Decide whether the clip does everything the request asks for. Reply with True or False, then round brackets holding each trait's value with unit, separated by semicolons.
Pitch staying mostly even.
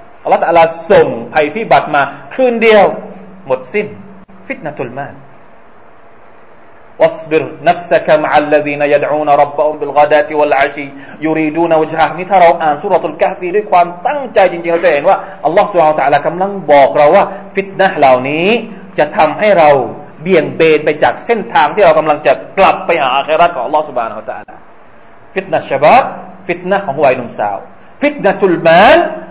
False (5.2 semitones)